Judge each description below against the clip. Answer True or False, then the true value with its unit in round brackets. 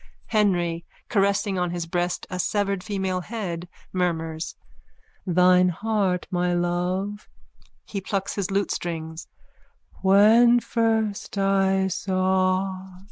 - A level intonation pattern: True (2.2 semitones)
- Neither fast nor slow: False (100 wpm)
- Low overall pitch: False (190 Hz)